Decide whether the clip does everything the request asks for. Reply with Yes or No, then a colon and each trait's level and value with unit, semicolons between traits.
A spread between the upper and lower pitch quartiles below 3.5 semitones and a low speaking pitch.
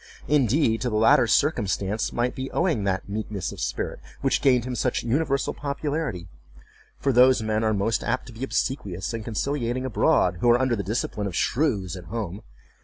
No: average, 4.2 semitones; low, 120 Hz